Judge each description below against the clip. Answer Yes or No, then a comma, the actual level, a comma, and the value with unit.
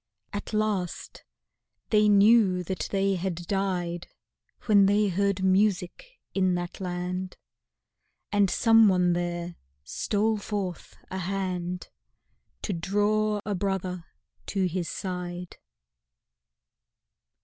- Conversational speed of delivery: No, slow, 100 wpm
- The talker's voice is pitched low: No, high, 190 Hz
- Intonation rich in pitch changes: No, narrow, 2.5 semitones